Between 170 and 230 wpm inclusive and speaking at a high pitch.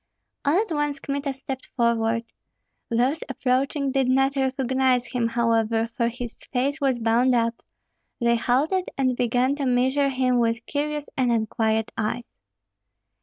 No: average, 140 wpm; very high, 255 Hz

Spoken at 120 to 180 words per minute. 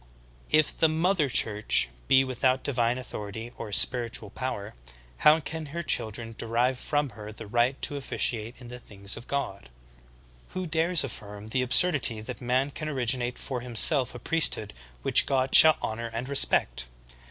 Yes: average, 165 wpm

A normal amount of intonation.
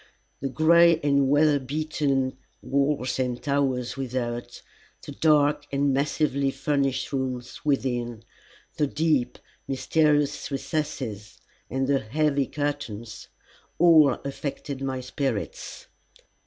No: narrow, 2.2 semitones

